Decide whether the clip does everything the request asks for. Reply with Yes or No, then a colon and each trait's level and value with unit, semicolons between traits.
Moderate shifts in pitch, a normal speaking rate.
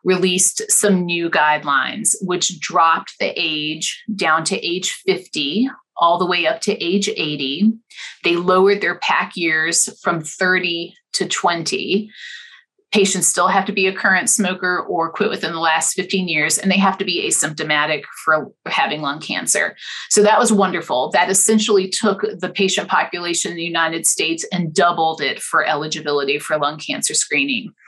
Yes: average, 4.0 semitones; average, 165 wpm